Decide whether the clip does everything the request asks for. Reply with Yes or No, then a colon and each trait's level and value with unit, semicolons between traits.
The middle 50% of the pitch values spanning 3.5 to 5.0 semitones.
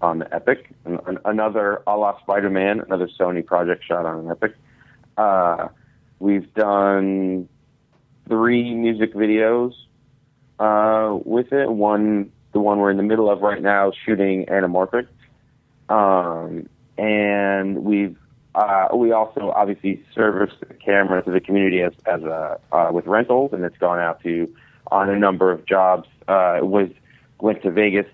No: average, 2.9 semitones